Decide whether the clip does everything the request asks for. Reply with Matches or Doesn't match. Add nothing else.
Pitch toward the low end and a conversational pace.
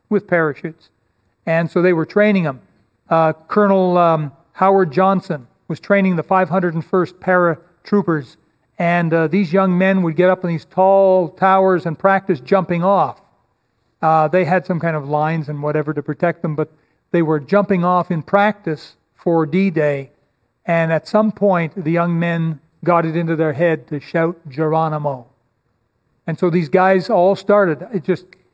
Doesn't match